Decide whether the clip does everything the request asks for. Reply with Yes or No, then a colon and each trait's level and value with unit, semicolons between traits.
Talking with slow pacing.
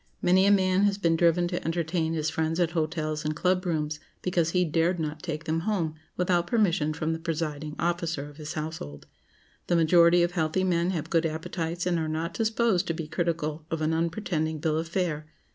No: average, 200 wpm